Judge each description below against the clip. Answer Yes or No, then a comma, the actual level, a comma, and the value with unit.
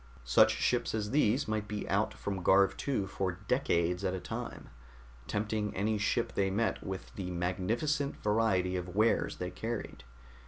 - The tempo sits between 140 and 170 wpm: Yes, average, 160 wpm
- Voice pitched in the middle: No, low, 105 Hz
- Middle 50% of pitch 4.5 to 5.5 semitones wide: No, average, 3.3 semitones